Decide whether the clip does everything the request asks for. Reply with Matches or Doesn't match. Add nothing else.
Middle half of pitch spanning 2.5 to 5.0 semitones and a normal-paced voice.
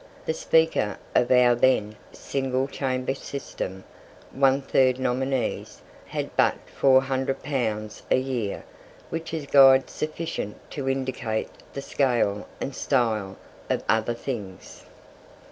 Doesn't match